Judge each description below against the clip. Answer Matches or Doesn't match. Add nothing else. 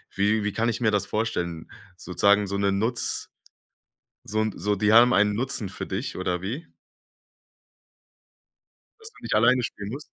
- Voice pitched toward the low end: Matches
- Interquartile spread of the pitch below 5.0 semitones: Matches